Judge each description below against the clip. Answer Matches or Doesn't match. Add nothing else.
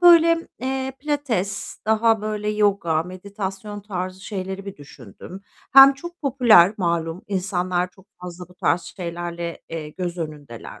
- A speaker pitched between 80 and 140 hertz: Doesn't match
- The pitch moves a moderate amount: Matches